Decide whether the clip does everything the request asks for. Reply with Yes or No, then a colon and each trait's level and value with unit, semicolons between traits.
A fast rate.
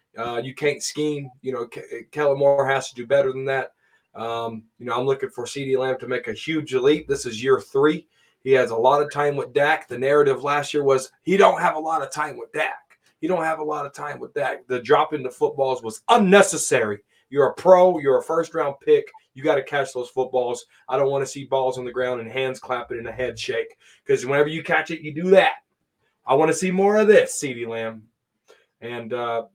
Yes: fast, 240 wpm